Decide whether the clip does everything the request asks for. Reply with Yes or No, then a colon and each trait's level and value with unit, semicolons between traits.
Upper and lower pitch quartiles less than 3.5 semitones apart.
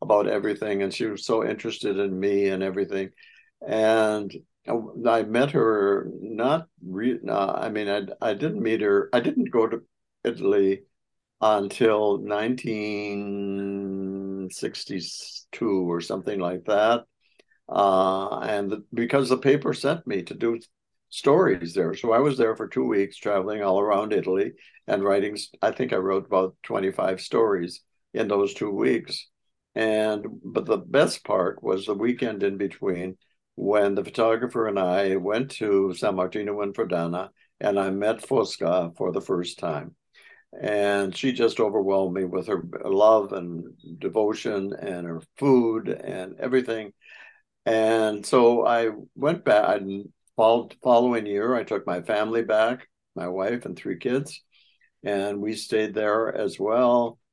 Yes: narrow, 2.4 semitones